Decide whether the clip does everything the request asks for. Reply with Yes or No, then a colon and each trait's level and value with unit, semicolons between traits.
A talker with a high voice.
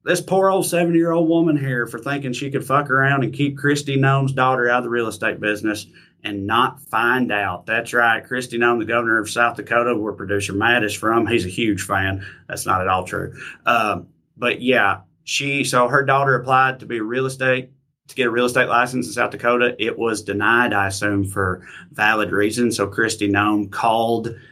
No: low, 120 Hz